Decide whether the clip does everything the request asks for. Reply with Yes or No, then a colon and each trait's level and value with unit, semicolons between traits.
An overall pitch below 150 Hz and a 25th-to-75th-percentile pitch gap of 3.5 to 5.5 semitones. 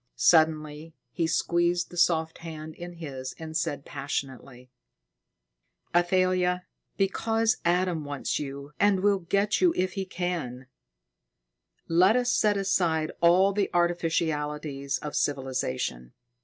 No: medium, 170 Hz; average, 3.8 semitones